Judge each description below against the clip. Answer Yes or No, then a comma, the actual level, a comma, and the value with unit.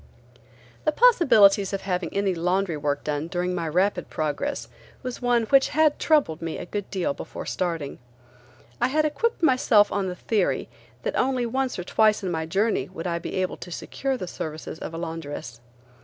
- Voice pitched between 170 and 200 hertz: Yes, high, 190 Hz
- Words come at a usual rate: Yes, average, 185 wpm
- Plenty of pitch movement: Yes, wide, 6.8 semitones